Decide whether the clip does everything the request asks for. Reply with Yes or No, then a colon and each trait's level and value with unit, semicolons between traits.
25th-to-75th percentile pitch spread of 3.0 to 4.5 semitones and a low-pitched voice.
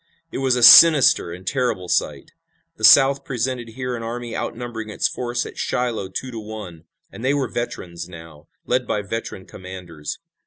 No: average, 5.2 semitones; low, 115 Hz